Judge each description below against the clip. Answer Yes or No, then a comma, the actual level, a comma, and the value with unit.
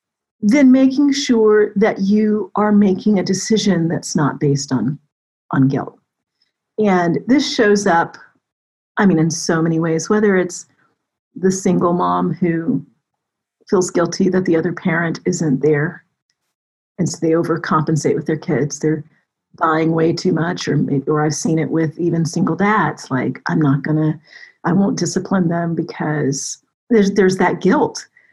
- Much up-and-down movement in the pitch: No, average, 4.3 semitones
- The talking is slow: No, average, 160 wpm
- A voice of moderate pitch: Yes, medium, 170 Hz